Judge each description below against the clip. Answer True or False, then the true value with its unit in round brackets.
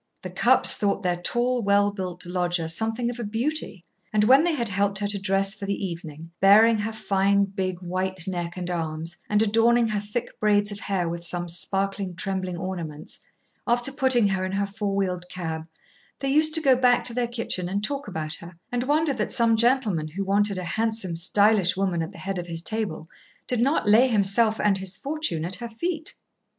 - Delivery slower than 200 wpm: False (205 wpm)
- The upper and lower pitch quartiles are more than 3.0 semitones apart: True (4.1 semitones)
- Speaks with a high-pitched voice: True (200 Hz)